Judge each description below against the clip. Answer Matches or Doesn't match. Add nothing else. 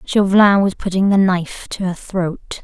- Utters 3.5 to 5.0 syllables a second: Matches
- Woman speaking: Matches